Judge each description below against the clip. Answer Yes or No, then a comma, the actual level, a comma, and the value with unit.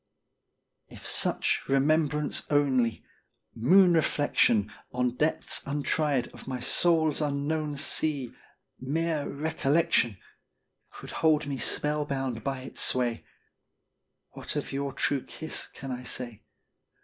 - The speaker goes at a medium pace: No, slow, 110 wpm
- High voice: No, medium, 140 Hz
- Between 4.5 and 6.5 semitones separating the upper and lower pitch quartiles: No, average, 3.2 semitones